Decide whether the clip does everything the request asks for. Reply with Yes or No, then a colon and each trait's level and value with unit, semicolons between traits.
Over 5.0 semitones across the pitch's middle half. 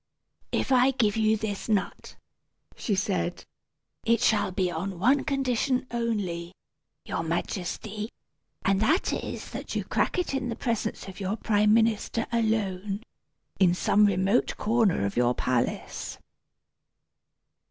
No: average, 3.5 semitones